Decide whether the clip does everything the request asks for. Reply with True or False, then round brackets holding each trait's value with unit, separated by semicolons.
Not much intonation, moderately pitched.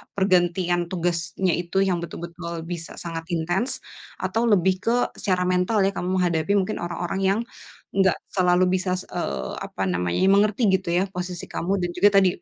True (1.9 semitones; 180 Hz)